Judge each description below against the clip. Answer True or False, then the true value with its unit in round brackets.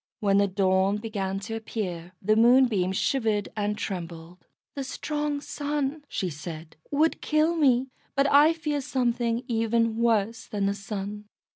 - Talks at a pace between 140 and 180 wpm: True (145 wpm)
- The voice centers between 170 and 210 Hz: False (225 Hz)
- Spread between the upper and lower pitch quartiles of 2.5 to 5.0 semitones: False (5.4 semitones)